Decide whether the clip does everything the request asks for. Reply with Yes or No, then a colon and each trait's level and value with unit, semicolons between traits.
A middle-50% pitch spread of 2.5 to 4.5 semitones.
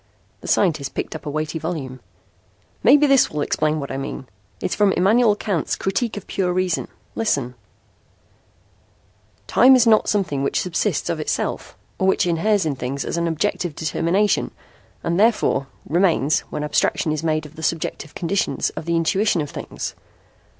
No: average, 4.9 semitones